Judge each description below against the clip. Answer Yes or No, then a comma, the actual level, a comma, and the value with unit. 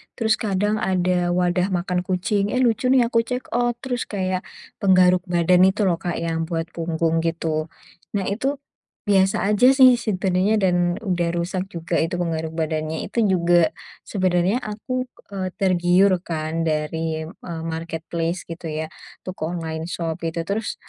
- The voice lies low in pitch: No, medium, 180 Hz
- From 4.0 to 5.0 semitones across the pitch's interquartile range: No, average, 3.2 semitones